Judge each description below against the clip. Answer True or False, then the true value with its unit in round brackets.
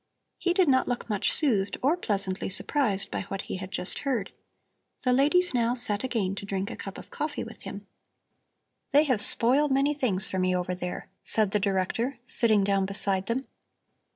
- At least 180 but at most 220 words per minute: True (190 wpm)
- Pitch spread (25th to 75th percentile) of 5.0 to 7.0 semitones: True (5.5 semitones)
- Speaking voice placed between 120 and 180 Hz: False (215 Hz)